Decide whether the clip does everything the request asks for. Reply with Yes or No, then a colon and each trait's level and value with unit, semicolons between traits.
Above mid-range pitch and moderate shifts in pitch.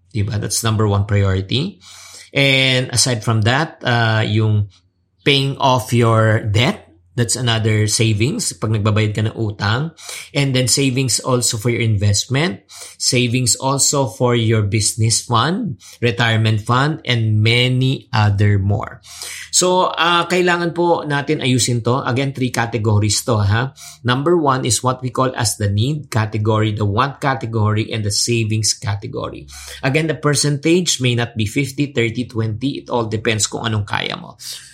No: low, 120 Hz; average, 3.6 semitones